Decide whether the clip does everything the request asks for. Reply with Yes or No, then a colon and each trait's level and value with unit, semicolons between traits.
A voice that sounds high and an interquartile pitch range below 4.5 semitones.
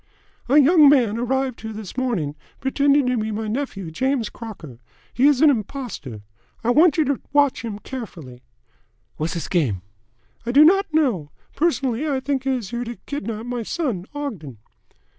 No: high, 245 Hz; average, 5.2 semitones